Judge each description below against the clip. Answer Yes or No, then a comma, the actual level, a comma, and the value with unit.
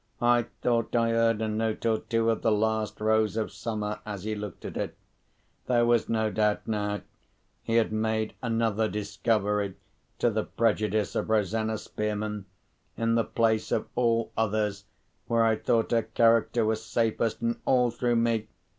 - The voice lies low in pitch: Yes, low, 110 Hz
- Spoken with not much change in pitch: Yes, narrow, 1.3 semitones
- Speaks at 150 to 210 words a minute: Yes, average, 165 wpm